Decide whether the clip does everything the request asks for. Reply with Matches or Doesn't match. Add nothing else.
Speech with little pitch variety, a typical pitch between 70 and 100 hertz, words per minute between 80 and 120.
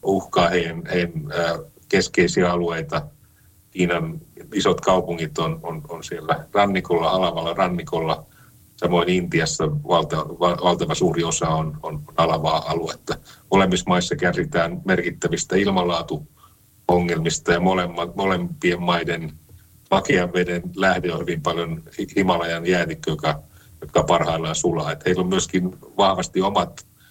Matches